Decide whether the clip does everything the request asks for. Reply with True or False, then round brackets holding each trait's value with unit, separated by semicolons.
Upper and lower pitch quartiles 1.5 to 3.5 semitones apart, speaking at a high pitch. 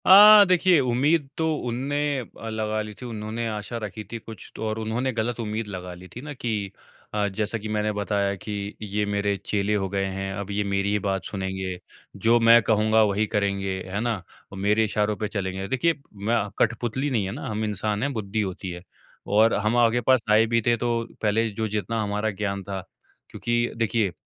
False (2.5 semitones; 105 Hz)